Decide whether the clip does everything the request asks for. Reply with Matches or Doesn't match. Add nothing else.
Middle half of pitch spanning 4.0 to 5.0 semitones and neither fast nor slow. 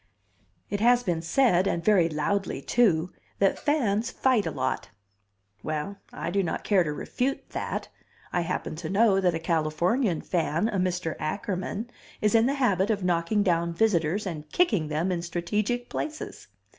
Matches